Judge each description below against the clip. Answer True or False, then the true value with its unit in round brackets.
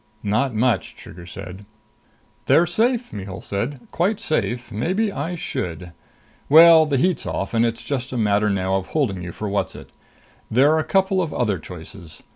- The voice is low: True (120 Hz)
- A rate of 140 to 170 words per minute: True (165 wpm)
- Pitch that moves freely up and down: True (8.3 semitones)